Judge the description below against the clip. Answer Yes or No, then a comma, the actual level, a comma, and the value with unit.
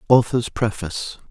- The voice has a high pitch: No, low, 110 Hz